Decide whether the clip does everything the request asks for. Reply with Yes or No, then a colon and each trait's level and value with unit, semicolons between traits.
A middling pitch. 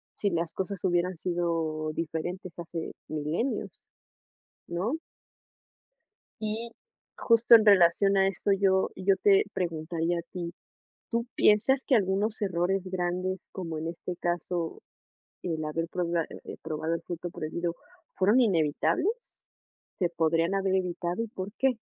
Yes: medium, 180 Hz